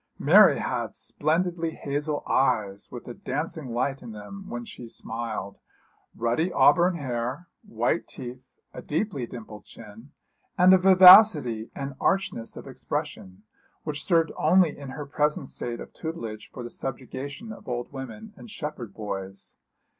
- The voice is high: No, low, 135 Hz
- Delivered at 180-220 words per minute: No, average, 145 wpm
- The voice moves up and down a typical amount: No, wide, 6.1 semitones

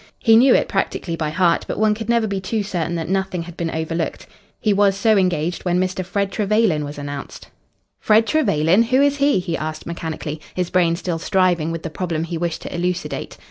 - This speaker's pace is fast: Yes, fast, 210 wpm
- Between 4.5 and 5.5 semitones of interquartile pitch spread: No, average, 3.8 semitones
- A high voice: No, medium, 180 Hz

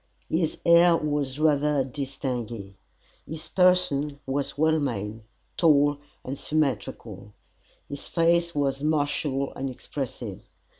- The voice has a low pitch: No, medium, 145 Hz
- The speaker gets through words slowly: Yes, slow, 105 wpm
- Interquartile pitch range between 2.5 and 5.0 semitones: Yes, average, 2.9 semitones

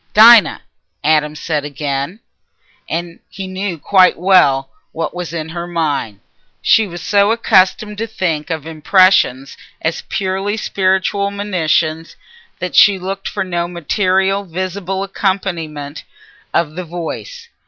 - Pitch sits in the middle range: Yes, medium, 180 Hz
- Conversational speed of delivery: No, slow, 120 wpm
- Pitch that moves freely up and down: No, average, 3.5 semitones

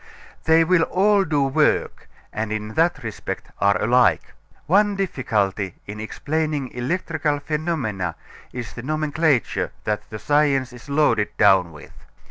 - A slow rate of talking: Yes, slow, 130 wpm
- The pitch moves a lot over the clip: Yes, wide, 6.8 semitones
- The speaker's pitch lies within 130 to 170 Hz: Yes, low, 135 Hz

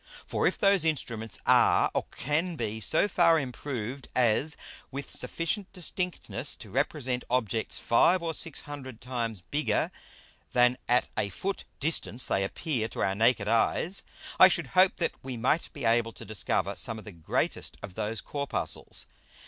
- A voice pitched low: Yes, low, 130 Hz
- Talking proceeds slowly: No, average, 160 wpm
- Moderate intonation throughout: No, wide, 6.1 semitones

